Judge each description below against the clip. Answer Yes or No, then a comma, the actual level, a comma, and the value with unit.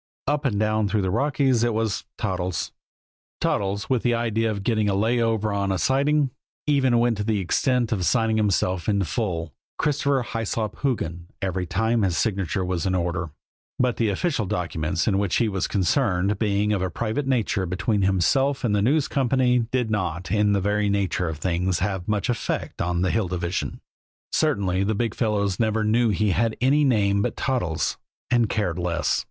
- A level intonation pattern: No, average, 4.1 semitones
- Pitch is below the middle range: Yes, low, 105 Hz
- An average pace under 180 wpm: No, average, 185 wpm